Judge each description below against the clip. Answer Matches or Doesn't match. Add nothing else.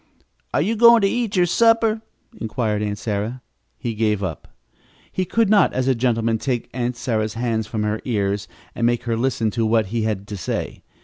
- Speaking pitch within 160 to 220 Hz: Doesn't match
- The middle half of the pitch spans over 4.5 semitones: Doesn't match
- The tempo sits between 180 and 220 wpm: Matches